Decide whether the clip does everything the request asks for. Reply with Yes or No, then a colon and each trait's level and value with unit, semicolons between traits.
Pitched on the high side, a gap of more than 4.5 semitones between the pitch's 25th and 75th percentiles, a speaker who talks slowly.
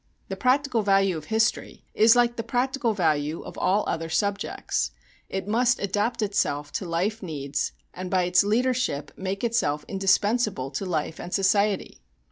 No: high, 195 Hz; average, 5.1 semitones; average, 155 wpm